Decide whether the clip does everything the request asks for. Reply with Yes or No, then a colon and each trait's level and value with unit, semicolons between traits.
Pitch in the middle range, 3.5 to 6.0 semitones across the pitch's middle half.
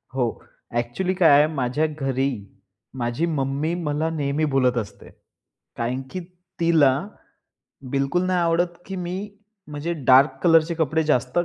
Yes: medium, 150 Hz; average, 4.0 semitones